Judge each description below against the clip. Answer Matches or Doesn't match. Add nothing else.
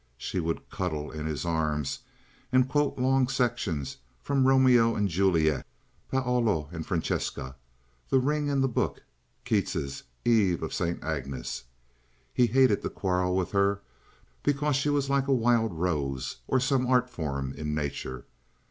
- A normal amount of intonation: Doesn't match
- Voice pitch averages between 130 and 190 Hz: Doesn't match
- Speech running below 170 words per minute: Matches